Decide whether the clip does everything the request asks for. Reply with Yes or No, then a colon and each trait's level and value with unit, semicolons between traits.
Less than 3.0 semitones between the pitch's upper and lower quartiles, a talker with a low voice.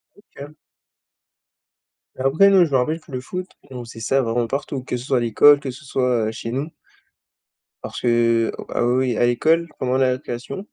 No: average, 3.3 semitones; low, 130 Hz